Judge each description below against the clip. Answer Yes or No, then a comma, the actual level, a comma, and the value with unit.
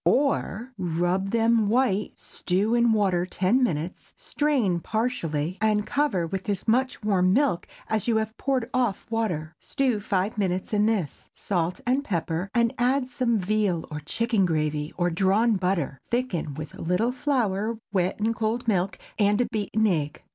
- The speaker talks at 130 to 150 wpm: No, average, 160 wpm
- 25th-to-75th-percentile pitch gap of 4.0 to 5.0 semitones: Yes, average, 4.7 semitones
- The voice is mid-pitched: No, high, 210 Hz